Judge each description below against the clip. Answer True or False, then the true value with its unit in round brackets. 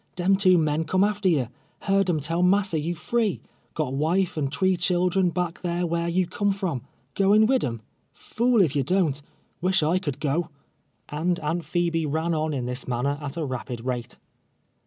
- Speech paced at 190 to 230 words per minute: True (200 wpm)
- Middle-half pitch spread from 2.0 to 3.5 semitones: False (4.1 semitones)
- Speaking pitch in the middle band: True (170 Hz)